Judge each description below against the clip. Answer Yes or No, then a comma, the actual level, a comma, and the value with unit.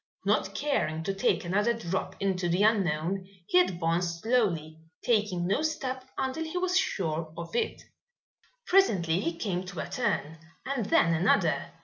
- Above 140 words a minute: Yes, average, 150 wpm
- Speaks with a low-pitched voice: No, high, 190 Hz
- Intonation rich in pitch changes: Yes, wide, 5.8 semitones